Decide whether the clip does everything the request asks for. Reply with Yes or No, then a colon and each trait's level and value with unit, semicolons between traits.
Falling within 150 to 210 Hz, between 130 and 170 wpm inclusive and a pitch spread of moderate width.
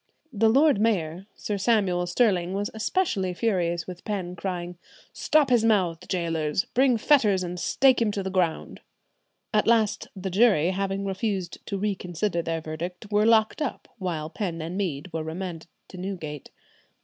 Yes: high, 190 Hz; average, 160 wpm; average, 3.7 semitones